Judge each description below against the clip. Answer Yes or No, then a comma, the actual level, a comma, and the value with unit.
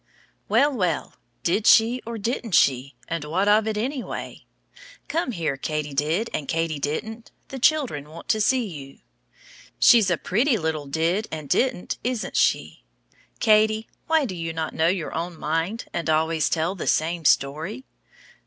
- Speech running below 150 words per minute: No, average, 160 wpm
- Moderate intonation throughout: No, wide, 6.1 semitones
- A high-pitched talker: No, medium, 175 Hz